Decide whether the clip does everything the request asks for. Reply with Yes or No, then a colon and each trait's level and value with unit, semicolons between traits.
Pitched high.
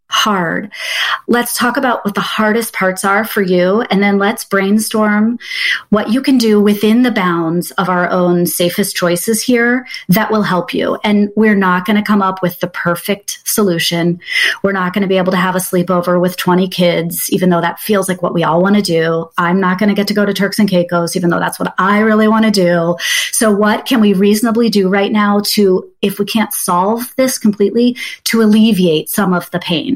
Yes: high, 200 Hz